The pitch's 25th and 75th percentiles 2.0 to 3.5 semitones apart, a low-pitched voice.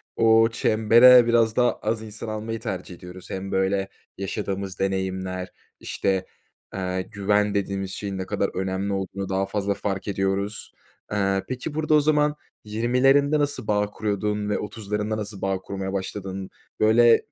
Yes: narrow, 2.6 semitones; low, 100 Hz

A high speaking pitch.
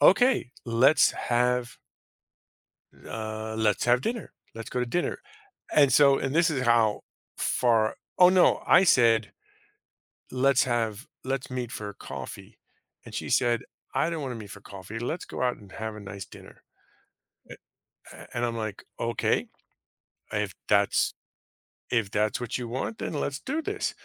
No: low, 120 Hz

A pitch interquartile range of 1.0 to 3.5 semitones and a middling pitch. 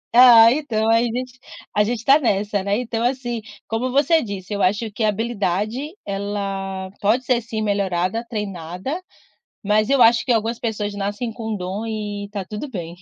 No: average, 3.1 semitones; high, 215 Hz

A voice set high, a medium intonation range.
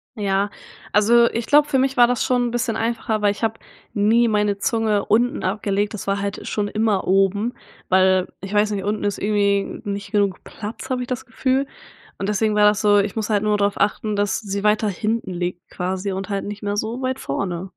No: high, 210 Hz; narrow, 2.1 semitones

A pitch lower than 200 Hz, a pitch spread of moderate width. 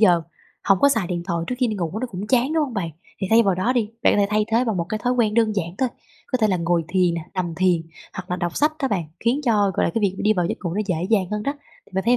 No: high, 205 Hz; average, 4.6 semitones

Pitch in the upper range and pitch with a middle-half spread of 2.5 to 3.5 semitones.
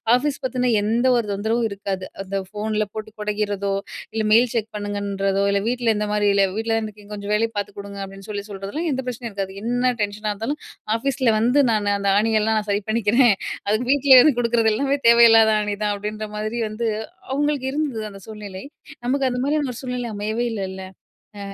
Yes: high, 215 Hz; average, 3.1 semitones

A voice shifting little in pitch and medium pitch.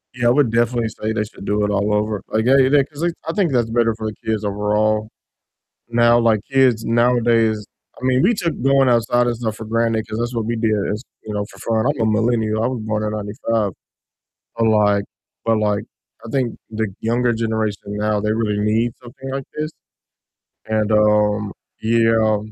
No: narrow, 2.0 semitones; low, 110 Hz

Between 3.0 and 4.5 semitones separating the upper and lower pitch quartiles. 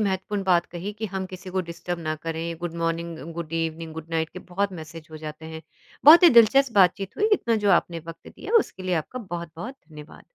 Yes: average, 3.3 semitones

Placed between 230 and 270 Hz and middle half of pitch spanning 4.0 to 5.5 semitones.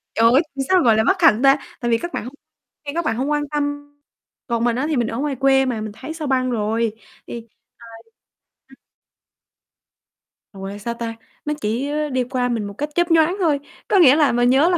Yes: very high, 260 Hz; average, 4.3 semitones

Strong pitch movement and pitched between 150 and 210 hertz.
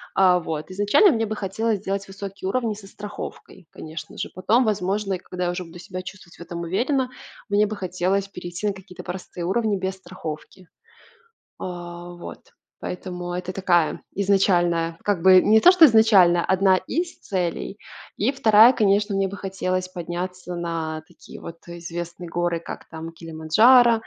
No: average, 2.8 semitones; medium, 185 Hz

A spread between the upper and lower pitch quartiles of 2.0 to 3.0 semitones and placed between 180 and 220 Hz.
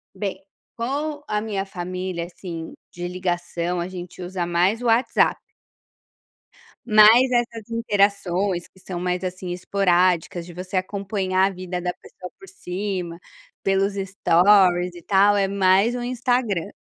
Yes: narrow, 2.6 semitones; high, 190 Hz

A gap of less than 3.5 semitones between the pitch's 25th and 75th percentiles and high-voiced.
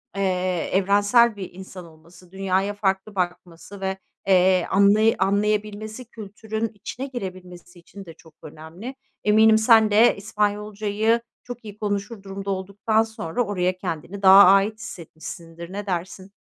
Yes: narrow, 2.5 semitones; high, 200 Hz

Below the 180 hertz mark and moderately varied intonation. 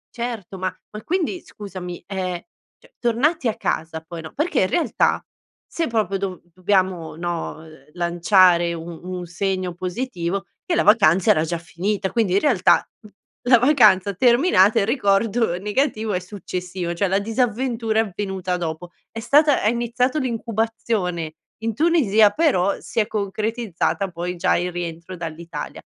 No: high, 195 Hz; average, 4.5 semitones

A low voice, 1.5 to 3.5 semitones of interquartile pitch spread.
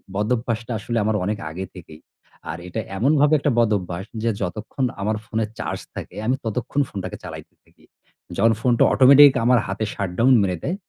No: low, 110 Hz; average, 4.4 semitones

